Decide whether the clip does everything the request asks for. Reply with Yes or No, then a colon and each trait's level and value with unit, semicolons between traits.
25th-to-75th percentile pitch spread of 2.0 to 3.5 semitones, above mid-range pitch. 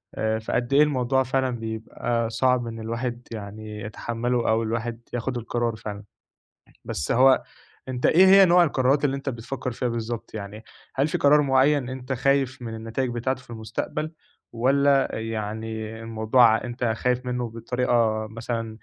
No: average, 2.8 semitones; low, 120 Hz